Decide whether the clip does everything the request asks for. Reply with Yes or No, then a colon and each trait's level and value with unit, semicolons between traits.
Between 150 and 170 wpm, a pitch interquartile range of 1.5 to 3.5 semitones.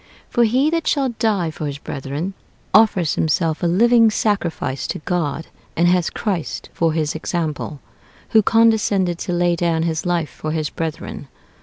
No: average, 160 wpm; average, 5.1 semitones